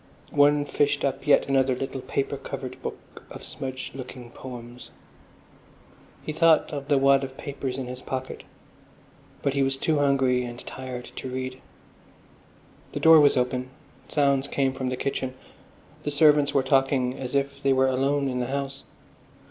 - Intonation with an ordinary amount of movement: No, narrow, 1.6 semitones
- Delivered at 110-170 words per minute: Yes, average, 165 wpm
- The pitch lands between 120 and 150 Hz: Yes, low, 135 Hz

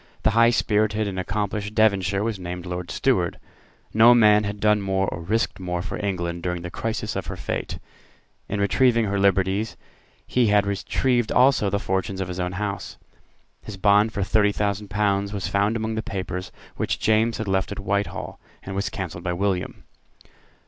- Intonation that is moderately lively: No, narrow, 2.1 semitones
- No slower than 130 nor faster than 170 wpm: No, average, 180 wpm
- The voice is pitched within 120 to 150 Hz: No, low, 100 Hz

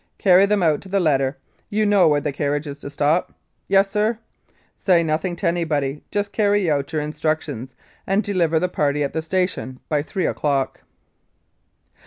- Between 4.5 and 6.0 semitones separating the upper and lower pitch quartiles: Yes, average, 4.9 semitones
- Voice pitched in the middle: Yes, medium, 160 Hz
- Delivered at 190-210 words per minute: No, average, 180 wpm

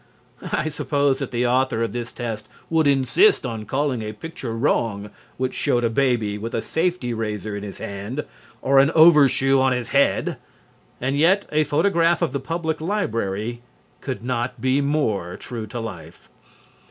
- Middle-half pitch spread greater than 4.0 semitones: Yes, average, 4.5 semitones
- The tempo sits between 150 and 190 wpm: Yes, average, 165 wpm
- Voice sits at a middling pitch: No, low, 130 Hz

